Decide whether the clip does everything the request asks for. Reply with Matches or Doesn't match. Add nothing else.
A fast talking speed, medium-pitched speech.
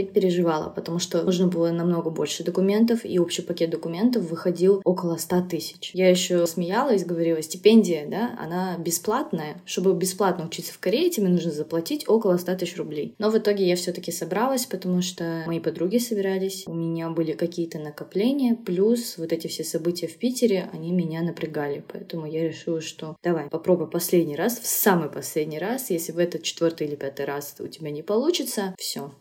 Matches